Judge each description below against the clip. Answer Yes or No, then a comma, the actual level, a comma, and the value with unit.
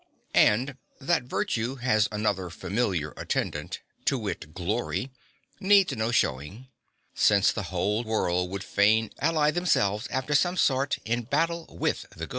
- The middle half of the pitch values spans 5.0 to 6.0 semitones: Yes, wide, 5.6 semitones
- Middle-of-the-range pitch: No, low, 110 Hz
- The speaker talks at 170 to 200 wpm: No, average, 140 wpm